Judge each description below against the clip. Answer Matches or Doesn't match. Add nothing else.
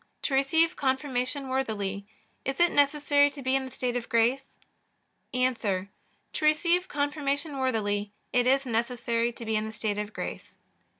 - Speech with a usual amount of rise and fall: Matches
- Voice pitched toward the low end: Doesn't match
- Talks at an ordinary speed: Matches